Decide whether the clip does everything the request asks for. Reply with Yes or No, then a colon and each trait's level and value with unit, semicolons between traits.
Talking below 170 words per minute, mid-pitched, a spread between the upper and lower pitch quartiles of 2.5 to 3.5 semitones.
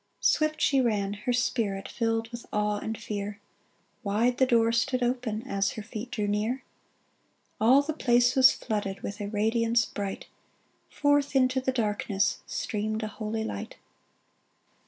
No: average, 155 wpm; high, 225 Hz; average, 3.2 semitones